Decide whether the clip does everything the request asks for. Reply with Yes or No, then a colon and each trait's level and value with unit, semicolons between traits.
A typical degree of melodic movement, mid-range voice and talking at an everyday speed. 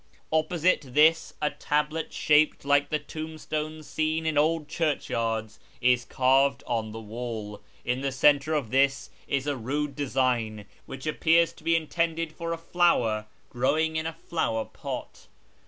Yes: average, 4.2 semitones; medium, 145 Hz; average, 150 wpm